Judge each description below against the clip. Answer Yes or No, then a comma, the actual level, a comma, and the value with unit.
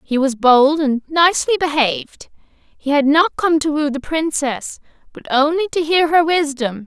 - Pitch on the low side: No, very high, 300 Hz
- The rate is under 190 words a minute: Yes, average, 175 wpm